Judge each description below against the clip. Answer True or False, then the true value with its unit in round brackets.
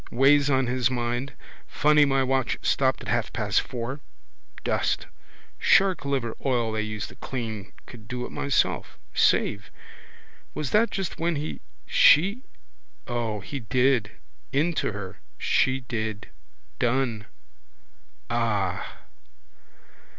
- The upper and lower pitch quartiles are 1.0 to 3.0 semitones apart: False (3.8 semitones)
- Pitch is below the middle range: True (125 Hz)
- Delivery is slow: True (120 wpm)